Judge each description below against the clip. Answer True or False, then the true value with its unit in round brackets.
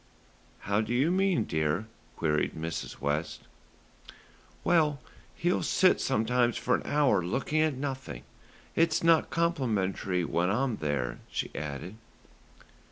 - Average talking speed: False (120 wpm)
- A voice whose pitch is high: False (120 Hz)